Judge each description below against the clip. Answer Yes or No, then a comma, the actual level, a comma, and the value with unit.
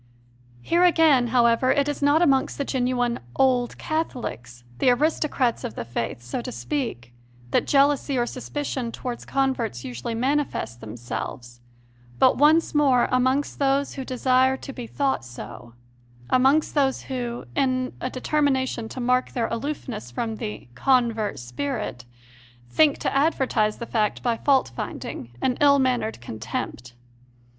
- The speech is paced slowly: No, average, 145 wpm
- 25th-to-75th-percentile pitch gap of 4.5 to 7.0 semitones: No, average, 3.8 semitones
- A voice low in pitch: No, very high, 255 Hz